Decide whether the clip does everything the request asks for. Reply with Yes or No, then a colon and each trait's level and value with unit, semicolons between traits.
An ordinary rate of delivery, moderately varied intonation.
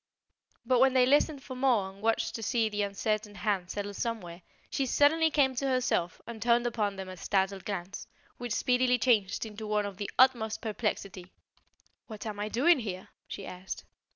Yes: average, 180 wpm; average, 3.9 semitones